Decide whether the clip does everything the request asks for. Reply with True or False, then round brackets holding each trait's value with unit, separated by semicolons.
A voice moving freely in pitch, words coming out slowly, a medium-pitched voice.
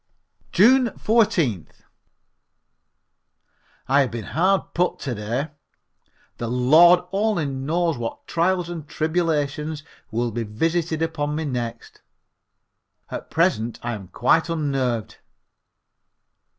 True (5.9 semitones; 105 wpm; 150 Hz)